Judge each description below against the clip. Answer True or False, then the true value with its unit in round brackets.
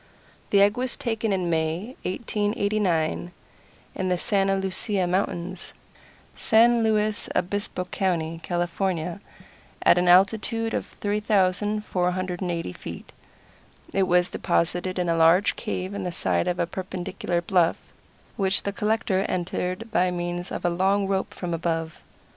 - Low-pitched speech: False (185 Hz)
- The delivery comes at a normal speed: False (130 wpm)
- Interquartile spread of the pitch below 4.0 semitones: True (2.7 semitones)